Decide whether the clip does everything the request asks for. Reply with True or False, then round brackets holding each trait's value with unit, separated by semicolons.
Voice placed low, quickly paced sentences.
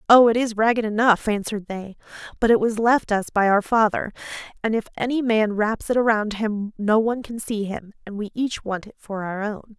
False (215 Hz; 220 wpm)